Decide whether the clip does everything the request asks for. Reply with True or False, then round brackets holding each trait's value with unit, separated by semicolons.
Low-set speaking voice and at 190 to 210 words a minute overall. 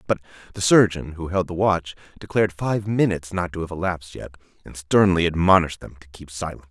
True (85 Hz; 195 wpm)